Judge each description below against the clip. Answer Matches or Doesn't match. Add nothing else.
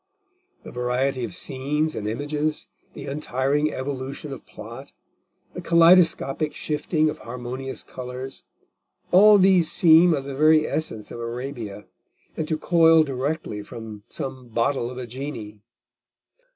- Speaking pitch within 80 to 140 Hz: Matches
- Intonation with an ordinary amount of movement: Matches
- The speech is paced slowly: Matches